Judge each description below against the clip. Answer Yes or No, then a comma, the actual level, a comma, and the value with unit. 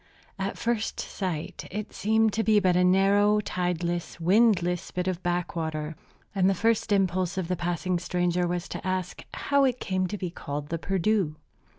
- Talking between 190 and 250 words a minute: No, average, 175 wpm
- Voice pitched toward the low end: No, medium, 185 Hz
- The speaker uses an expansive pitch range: No, average, 2.7 semitones